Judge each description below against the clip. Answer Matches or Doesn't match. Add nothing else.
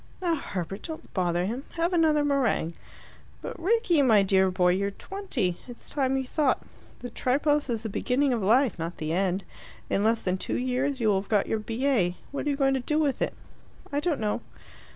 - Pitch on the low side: Doesn't match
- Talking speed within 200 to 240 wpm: Matches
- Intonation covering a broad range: Matches